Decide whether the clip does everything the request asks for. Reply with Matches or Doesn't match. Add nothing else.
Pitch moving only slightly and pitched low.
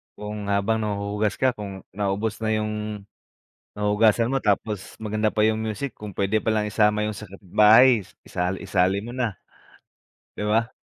Matches